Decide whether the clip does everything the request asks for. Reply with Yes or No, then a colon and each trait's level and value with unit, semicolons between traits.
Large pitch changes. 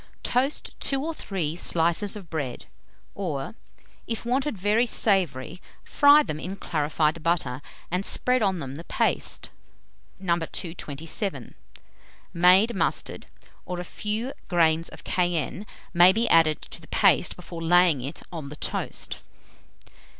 No: average, 4.5 semitones